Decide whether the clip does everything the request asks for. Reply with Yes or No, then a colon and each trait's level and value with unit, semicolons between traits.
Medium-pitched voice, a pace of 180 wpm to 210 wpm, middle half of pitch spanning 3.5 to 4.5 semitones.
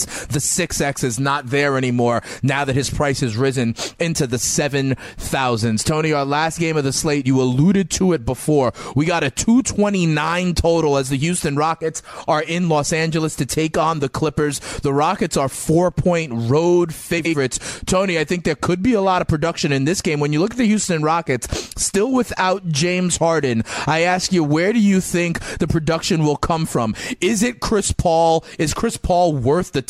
Yes: medium, 160 Hz; average, 195 wpm; average, 4.0 semitones